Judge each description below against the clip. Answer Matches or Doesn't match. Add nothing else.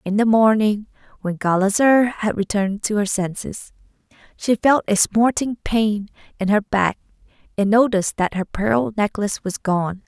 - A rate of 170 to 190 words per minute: Doesn't match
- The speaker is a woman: Matches